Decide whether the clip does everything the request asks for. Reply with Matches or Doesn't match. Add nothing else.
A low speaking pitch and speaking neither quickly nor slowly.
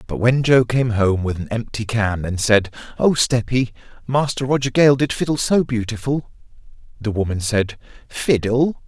Matches